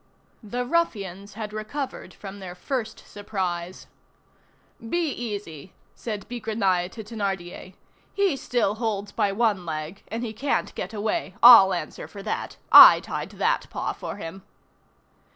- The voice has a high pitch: Yes, high, 205 Hz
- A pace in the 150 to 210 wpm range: No, slow, 135 wpm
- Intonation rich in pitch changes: No, average, 3.3 semitones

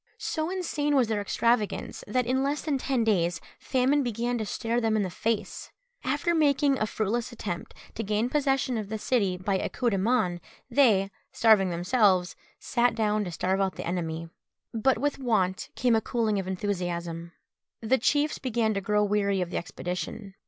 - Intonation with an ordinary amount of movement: Yes, average, 4.7 semitones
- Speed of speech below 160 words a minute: No, average, 180 wpm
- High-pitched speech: Yes, high, 220 Hz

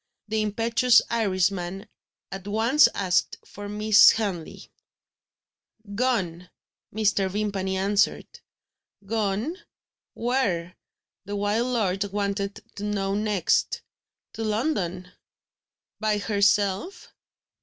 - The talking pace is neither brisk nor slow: No, slow, 90 wpm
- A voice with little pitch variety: Yes, narrow, 2.1 semitones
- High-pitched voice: Yes, high, 205 Hz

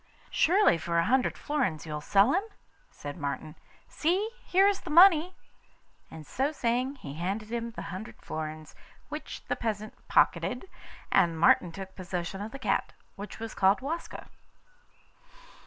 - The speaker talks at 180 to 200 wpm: No, average, 150 wpm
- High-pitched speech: Yes, high, 215 Hz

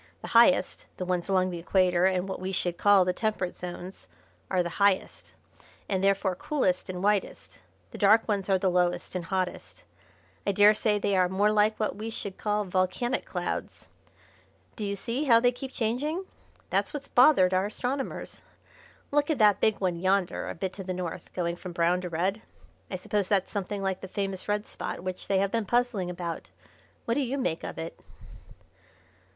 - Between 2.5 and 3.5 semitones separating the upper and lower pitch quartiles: Yes, average, 2.8 semitones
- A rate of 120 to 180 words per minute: No, average, 190 wpm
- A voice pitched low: No, high, 195 Hz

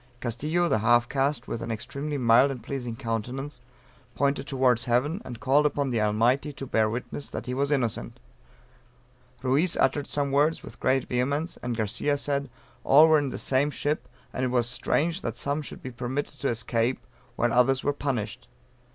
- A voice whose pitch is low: Yes, low, 130 Hz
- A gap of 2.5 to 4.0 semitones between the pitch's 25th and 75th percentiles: Yes, average, 3.1 semitones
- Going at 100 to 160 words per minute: No, average, 180 wpm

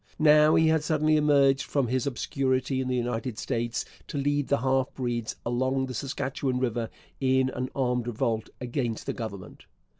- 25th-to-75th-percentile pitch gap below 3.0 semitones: Yes, narrow, 2.5 semitones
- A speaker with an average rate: Yes, average, 170 wpm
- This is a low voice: Yes, low, 130 Hz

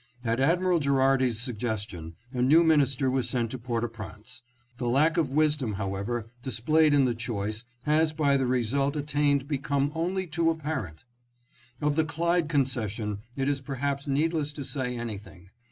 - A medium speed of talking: Yes, average, 170 wpm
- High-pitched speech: No, low, 135 Hz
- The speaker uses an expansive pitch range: No, average, 4.1 semitones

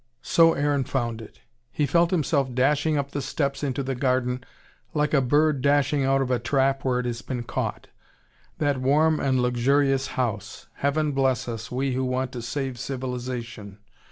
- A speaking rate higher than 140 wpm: Yes, average, 175 wpm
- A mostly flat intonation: Yes, narrow, 2.3 semitones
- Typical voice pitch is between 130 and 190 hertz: Yes, low, 135 Hz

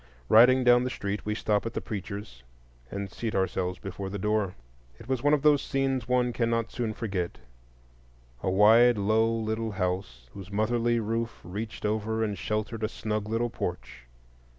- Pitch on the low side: Yes, low, 110 Hz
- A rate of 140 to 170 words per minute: Yes, average, 165 wpm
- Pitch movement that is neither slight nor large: Yes, average, 3.4 semitones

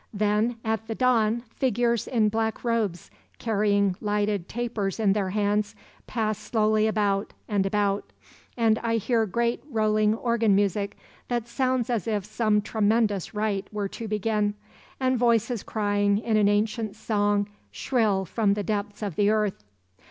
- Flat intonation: Yes, narrow, 1.9 semitones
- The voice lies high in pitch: Yes, high, 215 Hz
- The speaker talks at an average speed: Yes, average, 150 wpm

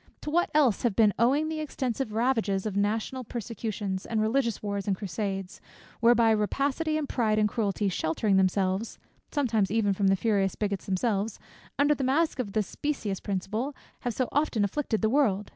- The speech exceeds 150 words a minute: Yes, average, 175 wpm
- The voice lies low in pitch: No, high, 220 Hz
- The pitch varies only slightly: No, average, 4.4 semitones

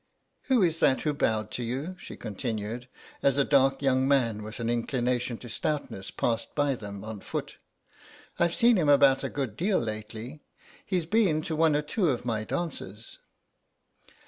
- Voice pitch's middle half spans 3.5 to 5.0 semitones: No, wide, 5.4 semitones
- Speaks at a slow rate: No, average, 170 wpm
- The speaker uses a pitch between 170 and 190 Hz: No, low, 130 Hz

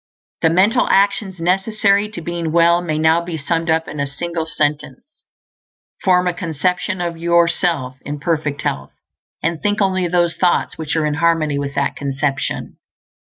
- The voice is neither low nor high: Yes, medium, 170 Hz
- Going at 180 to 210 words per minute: No, average, 160 wpm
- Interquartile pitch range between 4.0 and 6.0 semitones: No, average, 2.8 semitones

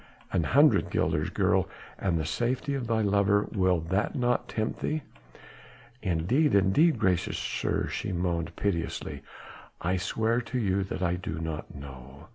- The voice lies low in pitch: Yes, very low, 95 Hz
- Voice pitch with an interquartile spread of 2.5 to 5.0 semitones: No, wide, 5.4 semitones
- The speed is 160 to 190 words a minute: No, average, 150 wpm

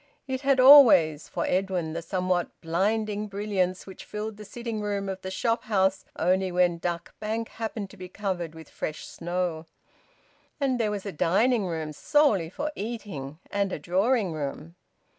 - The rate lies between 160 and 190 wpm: Yes, average, 165 wpm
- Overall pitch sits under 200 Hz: Yes, high, 190 Hz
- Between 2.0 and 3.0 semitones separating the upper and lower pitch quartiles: No, average, 3.9 semitones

